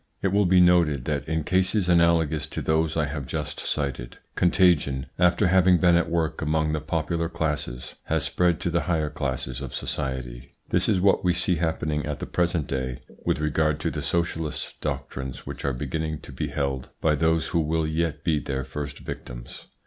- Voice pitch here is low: Yes, very low, 80 Hz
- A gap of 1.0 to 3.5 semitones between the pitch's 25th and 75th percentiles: Yes, average, 3.1 semitones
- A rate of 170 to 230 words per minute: Yes, average, 190 wpm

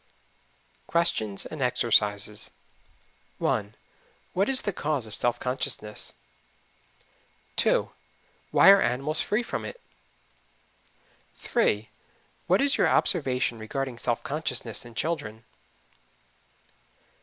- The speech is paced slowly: Yes, slow, 100 wpm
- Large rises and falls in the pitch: Yes, wide, 6.4 semitones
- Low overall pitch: Yes, low, 125 Hz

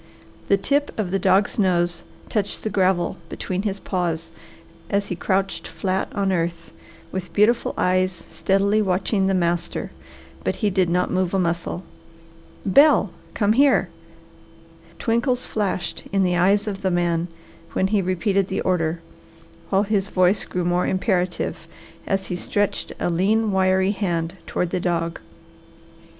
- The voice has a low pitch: No, high, 190 Hz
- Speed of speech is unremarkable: Yes, average, 145 wpm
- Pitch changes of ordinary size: No, narrow, 2.1 semitones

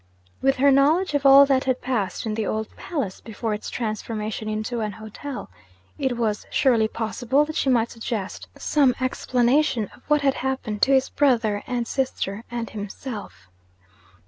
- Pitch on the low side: No, high, 240 Hz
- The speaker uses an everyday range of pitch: Yes, average, 3.9 semitones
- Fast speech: No, average, 165 wpm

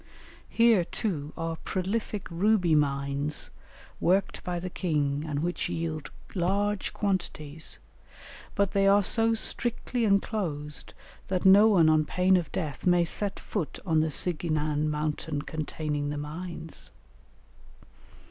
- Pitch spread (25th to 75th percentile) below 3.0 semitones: No, average, 4.6 semitones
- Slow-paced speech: Yes, slow, 125 wpm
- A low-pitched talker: No, medium, 170 Hz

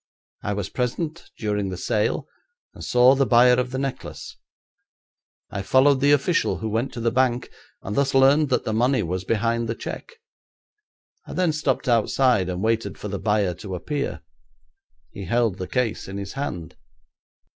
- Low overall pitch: Yes, low, 115 Hz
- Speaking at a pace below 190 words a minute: Yes, average, 170 wpm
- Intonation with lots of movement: No, average, 4.5 semitones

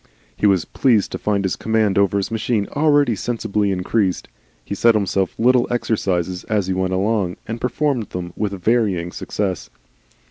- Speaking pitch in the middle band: No, low, 105 Hz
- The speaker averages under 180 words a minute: Yes, average, 165 wpm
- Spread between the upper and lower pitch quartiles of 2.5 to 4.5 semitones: Yes, average, 3.4 semitones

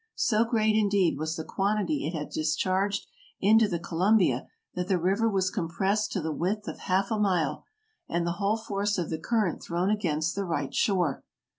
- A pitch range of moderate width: Yes, average, 3.8 semitones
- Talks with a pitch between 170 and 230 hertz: Yes, high, 190 Hz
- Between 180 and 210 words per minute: Yes, average, 190 wpm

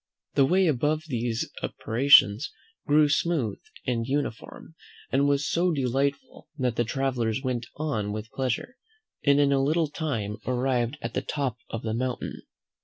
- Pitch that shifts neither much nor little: Yes, average, 3.7 semitones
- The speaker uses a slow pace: No, average, 150 wpm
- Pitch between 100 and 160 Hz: Yes, low, 135 Hz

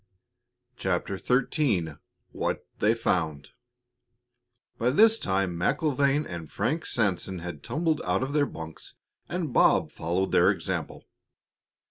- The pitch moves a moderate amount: No, wide, 9.0 semitones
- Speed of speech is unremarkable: No, slow, 115 wpm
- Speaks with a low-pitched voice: Yes, low, 110 Hz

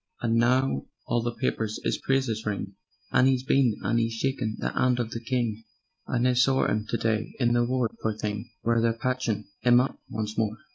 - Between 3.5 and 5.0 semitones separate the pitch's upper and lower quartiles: No, narrow, 2.4 semitones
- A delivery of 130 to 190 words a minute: No, fast, 205 wpm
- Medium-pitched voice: No, low, 115 Hz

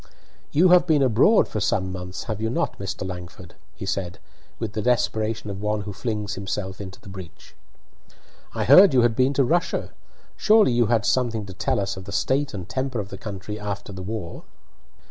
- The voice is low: Yes, low, 105 Hz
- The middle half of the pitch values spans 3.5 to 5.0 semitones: Yes, average, 4.3 semitones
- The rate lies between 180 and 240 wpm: Yes, average, 200 wpm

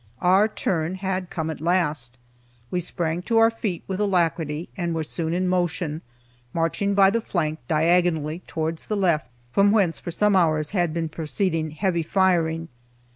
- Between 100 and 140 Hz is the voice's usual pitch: No, medium, 170 Hz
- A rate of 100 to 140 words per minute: No, average, 165 wpm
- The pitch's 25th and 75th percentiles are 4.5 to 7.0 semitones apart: No, average, 2.9 semitones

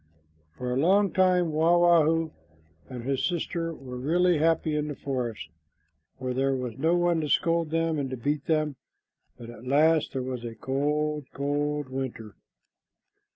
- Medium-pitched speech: Yes, medium, 150 Hz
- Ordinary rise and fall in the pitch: Yes, average, 4.0 semitones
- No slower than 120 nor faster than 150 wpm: No, average, 165 wpm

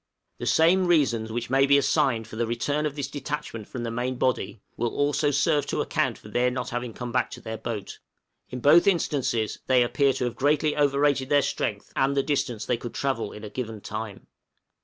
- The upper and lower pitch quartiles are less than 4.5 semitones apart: Yes, average, 3.6 semitones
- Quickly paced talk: Yes, fast, 210 wpm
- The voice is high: No, low, 130 Hz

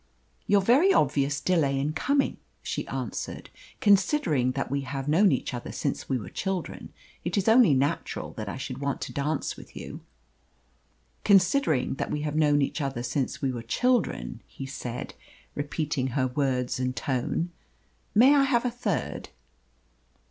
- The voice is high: No, medium, 145 Hz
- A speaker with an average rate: Yes, average, 160 wpm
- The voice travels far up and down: Yes, wide, 6.6 semitones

